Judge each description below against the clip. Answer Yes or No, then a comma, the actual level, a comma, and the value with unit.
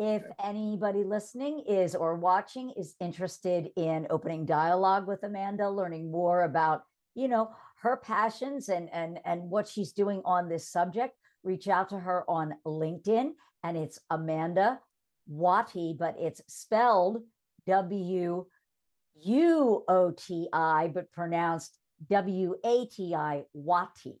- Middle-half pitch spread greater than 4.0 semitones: No, average, 3.7 semitones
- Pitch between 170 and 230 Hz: Yes, medium, 185 Hz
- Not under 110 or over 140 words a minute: Yes, slow, 135 wpm